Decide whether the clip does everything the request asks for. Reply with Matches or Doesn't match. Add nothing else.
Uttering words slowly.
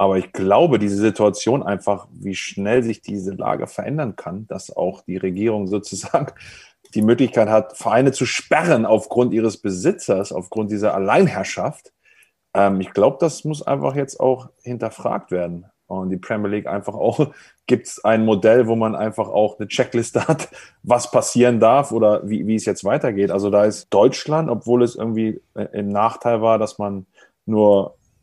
Doesn't match